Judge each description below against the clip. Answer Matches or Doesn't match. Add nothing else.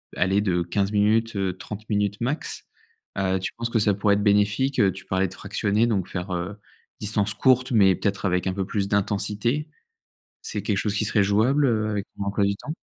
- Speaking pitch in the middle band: Doesn't match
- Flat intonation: Matches